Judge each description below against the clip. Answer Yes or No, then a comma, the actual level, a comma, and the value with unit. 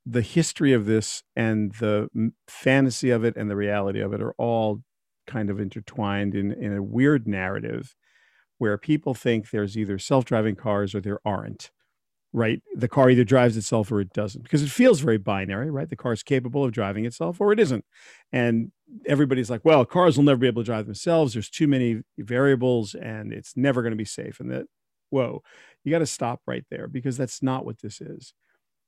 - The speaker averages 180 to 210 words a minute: Yes, fast, 205 wpm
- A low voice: Yes, low, 120 Hz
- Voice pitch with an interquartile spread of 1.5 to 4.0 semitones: No, average, 4.5 semitones